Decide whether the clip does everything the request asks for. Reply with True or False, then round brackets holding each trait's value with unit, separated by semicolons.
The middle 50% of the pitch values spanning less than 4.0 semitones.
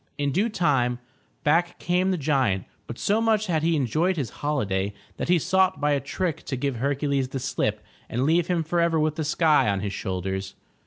False (5.3 semitones)